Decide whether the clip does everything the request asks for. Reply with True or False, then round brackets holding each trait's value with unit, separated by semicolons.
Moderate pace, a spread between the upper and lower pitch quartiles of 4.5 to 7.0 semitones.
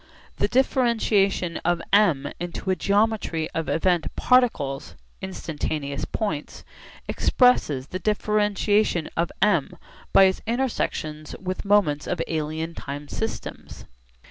False (110 wpm; 5.2 semitones)